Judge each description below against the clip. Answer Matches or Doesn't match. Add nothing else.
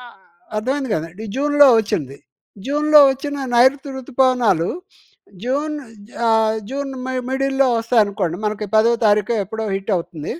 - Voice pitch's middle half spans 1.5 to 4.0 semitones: Doesn't match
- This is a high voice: Matches